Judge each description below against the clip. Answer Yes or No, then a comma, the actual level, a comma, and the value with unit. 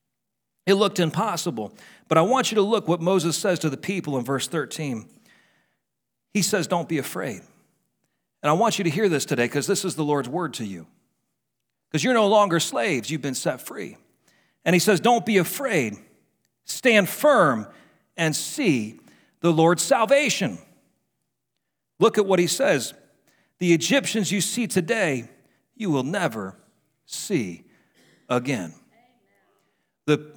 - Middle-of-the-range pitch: Yes, medium, 175 Hz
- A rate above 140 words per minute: Yes, average, 150 wpm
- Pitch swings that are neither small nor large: No, wide, 5.9 semitones